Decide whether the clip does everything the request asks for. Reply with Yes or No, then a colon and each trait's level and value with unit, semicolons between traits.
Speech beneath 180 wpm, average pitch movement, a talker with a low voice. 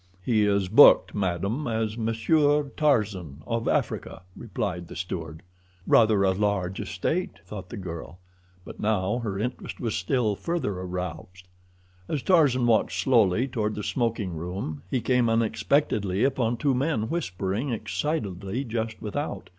Yes: average, 140 wpm; average, 4.9 semitones; low, 110 Hz